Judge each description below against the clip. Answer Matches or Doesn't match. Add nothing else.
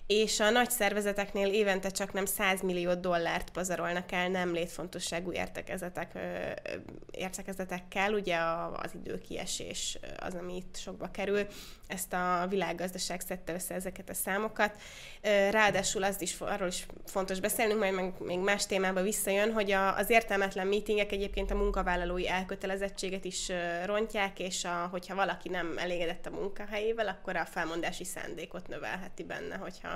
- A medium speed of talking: Matches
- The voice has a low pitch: Doesn't match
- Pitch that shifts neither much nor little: Doesn't match